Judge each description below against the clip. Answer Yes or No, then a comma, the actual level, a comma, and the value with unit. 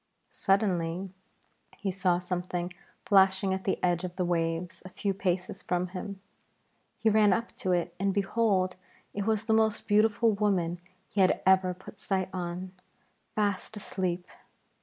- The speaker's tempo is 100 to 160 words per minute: Yes, average, 150 wpm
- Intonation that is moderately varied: No, narrow, 2.2 semitones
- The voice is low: No, high, 190 Hz